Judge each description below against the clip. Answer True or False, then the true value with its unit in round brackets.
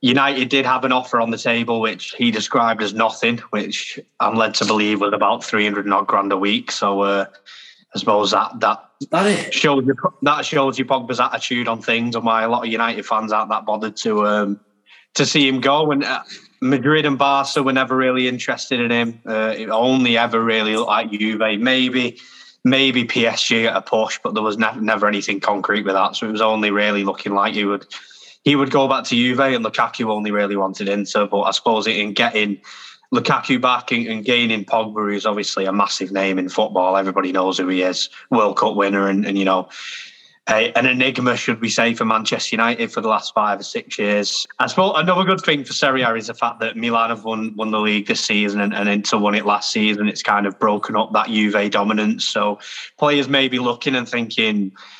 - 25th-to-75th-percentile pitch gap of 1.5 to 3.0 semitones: False (3.5 semitones)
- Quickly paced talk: True (220 wpm)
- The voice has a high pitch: False (110 Hz)